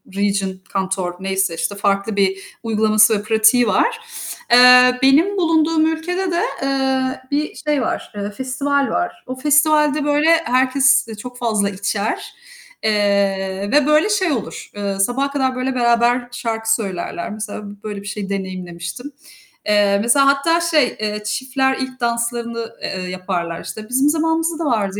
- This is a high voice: Yes, high, 235 Hz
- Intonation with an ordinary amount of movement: No, wide, 5.7 semitones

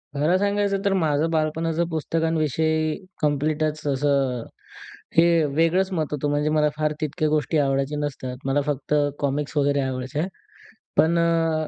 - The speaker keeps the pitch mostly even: Yes, narrow, 2.2 semitones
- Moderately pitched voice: Yes, medium, 155 Hz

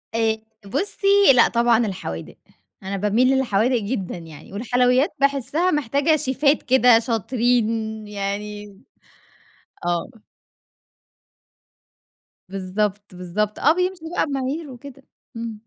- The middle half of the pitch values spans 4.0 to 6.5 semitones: Yes, average, 4.7 semitones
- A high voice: Yes, high, 230 Hz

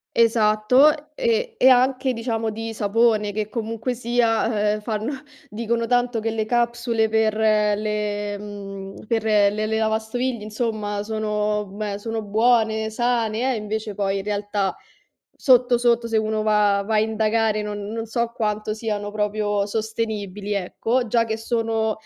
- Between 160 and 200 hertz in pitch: No, high, 220 Hz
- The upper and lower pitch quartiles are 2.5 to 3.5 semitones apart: No, narrow, 1.8 semitones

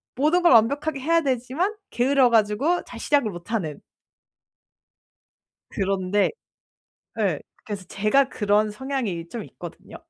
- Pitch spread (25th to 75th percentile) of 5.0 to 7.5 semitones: Yes, average, 5.3 semitones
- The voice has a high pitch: Yes, high, 235 Hz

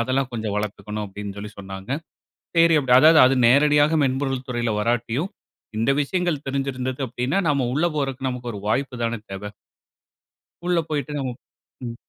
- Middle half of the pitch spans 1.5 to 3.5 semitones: No, average, 4.1 semitones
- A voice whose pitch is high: No, low, 130 Hz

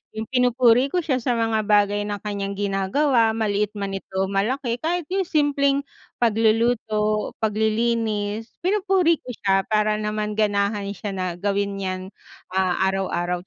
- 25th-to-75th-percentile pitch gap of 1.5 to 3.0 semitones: No, average, 3.4 semitones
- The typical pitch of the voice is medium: No, high, 215 Hz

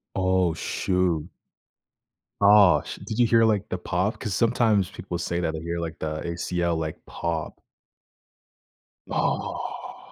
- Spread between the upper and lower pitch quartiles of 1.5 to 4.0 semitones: Yes, average, 3.2 semitones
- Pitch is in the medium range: No, very low, 90 Hz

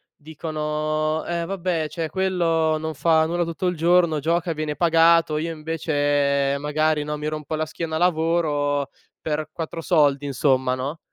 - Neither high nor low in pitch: Yes, medium, 155 Hz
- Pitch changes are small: Yes, narrow, 1.9 semitones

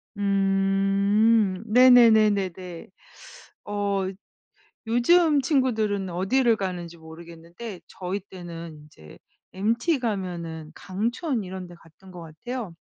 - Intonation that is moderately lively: Yes, average, 4.4 semitones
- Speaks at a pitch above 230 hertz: No, high, 195 Hz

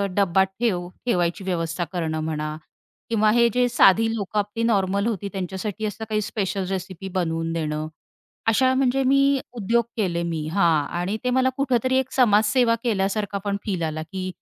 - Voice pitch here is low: No, high, 200 Hz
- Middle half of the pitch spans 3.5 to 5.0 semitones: Yes, average, 4.7 semitones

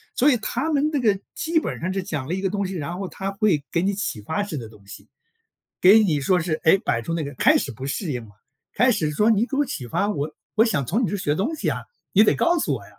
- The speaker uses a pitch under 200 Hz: Yes, high, 190 Hz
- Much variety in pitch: Yes, wide, 6.4 semitones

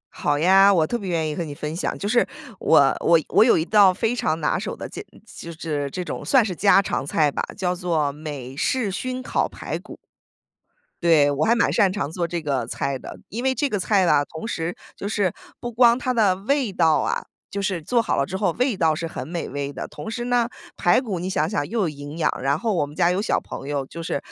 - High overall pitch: No, medium, 175 Hz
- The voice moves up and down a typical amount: No, wide, 6.1 semitones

